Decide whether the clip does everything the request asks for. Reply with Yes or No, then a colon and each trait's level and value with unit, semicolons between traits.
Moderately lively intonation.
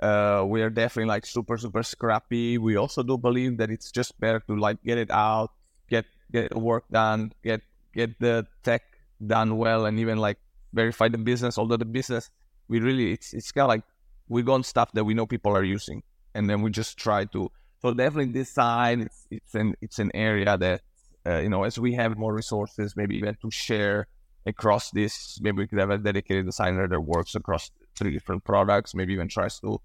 No: narrow, 2.1 semitones